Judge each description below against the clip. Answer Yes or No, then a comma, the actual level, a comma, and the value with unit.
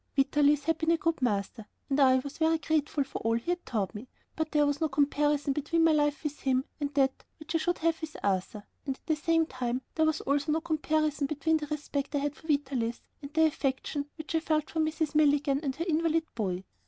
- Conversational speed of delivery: No, fast, 230 wpm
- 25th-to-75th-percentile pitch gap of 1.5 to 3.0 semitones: Yes, average, 2.7 semitones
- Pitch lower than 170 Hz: No, very high, 295 Hz